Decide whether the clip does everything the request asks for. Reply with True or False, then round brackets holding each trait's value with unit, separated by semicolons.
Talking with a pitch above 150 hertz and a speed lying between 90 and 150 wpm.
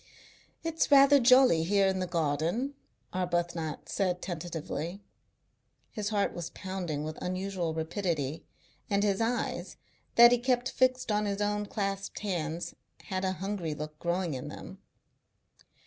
True (190 Hz; 135 wpm)